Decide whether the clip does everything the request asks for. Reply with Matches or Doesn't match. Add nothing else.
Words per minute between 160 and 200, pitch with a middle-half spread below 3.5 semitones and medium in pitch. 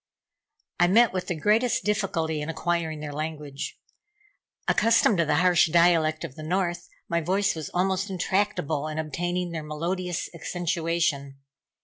Doesn't match